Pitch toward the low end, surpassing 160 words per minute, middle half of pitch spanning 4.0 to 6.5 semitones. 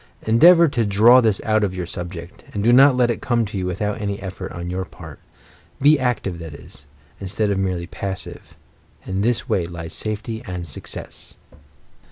Yes: low, 100 Hz; average, 185 wpm; average, 4.3 semitones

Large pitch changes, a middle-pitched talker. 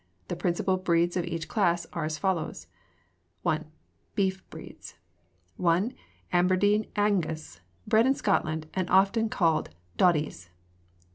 No: average, 3.2 semitones; medium, 180 Hz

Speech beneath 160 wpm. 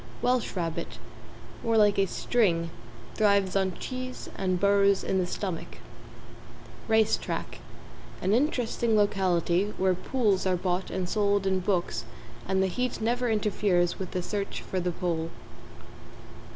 Yes: average, 140 wpm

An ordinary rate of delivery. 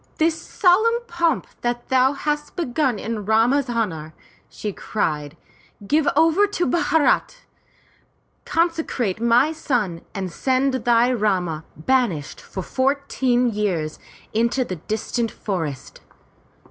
No: slow, 110 wpm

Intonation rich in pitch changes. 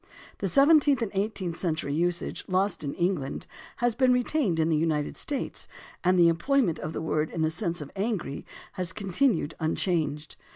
Yes: wide, 5.7 semitones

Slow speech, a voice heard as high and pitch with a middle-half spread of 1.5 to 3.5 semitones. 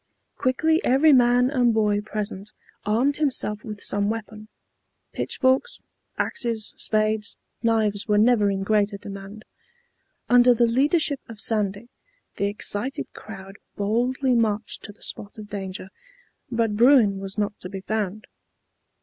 Yes: slow, 130 wpm; high, 215 Hz; average, 3.1 semitones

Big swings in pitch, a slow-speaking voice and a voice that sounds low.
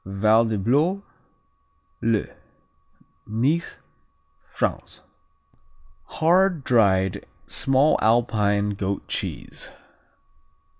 Yes: wide, 5.9 semitones; slow, 55 wpm; low, 115 Hz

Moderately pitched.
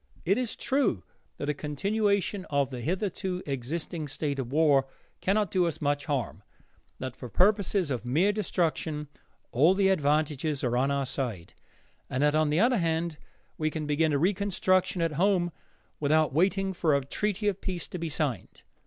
Yes: medium, 160 Hz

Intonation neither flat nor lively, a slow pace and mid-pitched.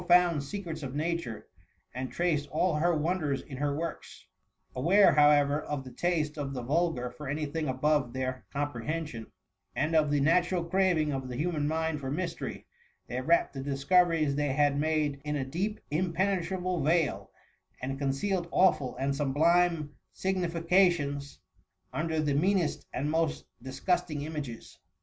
No: average, 3.5 semitones; average, 160 wpm; medium, 150 Hz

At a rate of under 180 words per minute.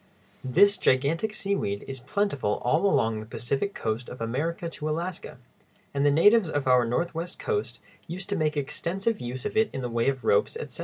No: average, 190 wpm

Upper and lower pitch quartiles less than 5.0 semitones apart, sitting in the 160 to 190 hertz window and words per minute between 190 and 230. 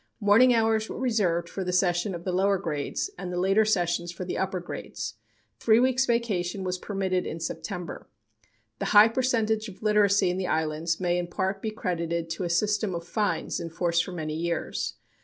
Yes: average, 3.6 semitones; medium, 185 Hz; average, 195 wpm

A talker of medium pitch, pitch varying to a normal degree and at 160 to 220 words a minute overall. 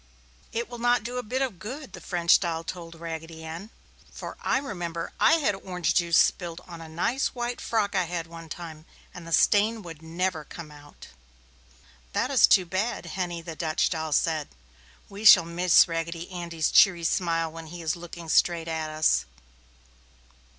Yes: medium, 170 Hz; average, 3.4 semitones; average, 180 wpm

